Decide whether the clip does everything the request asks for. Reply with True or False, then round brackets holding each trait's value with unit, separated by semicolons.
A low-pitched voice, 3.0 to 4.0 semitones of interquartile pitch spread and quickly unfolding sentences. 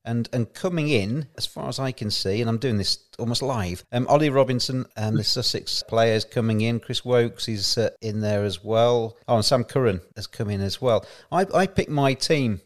True (115 Hz; 3.3 semitones; 230 wpm)